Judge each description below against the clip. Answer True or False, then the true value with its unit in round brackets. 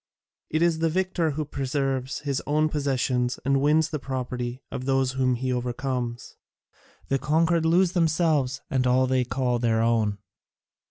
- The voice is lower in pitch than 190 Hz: True (135 Hz)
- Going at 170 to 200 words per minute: False (155 wpm)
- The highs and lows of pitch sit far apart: False (3.6 semitones)